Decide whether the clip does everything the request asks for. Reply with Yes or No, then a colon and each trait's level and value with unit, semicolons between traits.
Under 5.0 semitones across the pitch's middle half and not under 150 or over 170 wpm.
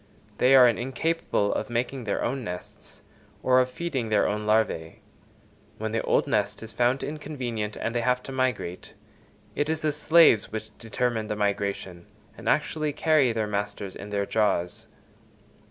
Yes: average, 4.0 semitones; average, 160 wpm